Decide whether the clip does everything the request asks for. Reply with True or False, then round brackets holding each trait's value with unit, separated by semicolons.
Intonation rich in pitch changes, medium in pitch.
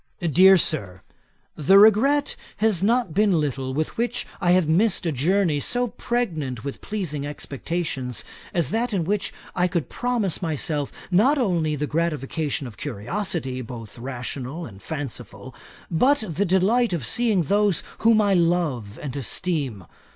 True (6.5 semitones; 170 Hz)